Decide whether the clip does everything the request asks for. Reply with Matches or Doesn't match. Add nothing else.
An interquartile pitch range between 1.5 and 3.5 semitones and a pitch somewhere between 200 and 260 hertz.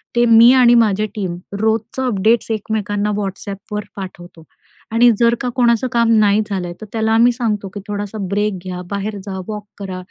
Matches